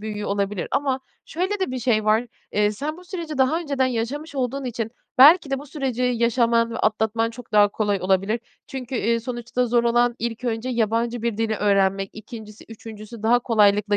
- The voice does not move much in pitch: No, average, 3.2 semitones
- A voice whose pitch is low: No, high, 230 Hz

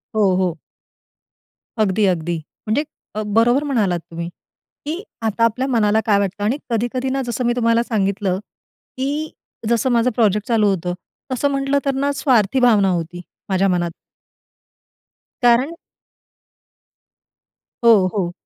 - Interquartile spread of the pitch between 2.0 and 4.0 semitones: No, average, 4.5 semitones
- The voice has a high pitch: Yes, high, 225 Hz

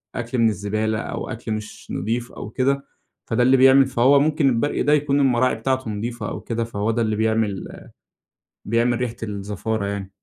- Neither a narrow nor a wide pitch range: Yes, average, 3.3 semitones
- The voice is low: Yes, low, 115 Hz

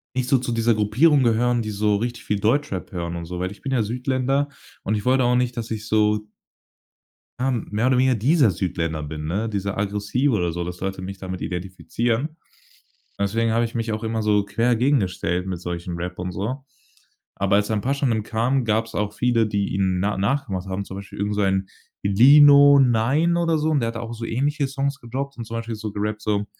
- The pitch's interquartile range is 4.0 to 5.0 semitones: Yes, average, 4.3 semitones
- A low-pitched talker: Yes, low, 110 Hz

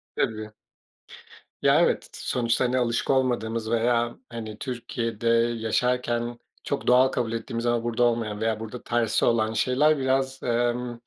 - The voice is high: No, low, 120 Hz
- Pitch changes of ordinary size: No, narrow, 1.5 semitones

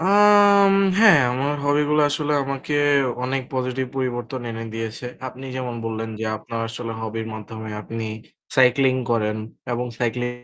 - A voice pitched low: Yes, low, 125 Hz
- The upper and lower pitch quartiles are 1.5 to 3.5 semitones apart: No, average, 3.9 semitones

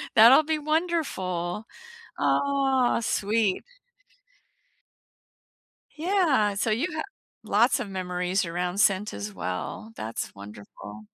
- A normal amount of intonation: No, wide, 7.3 semitones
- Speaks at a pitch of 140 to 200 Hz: No, high, 210 Hz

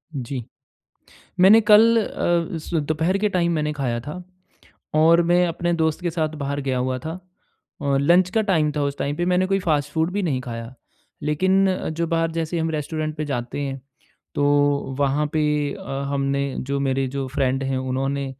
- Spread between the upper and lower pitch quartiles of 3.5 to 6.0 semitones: Yes, average, 4.0 semitones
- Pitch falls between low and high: Yes, medium, 150 Hz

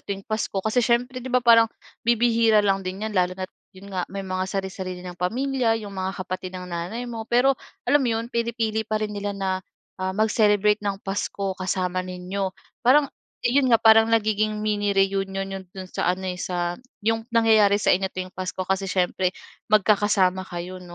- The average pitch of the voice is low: No, high, 200 Hz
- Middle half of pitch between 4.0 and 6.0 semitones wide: No, average, 3.1 semitones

